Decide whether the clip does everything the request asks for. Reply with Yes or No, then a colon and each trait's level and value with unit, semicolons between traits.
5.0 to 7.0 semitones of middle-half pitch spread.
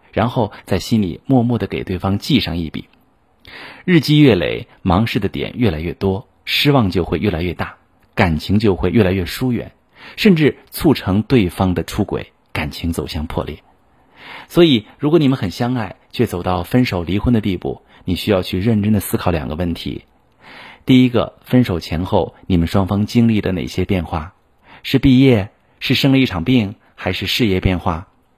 Yes: wide, 5.4 semitones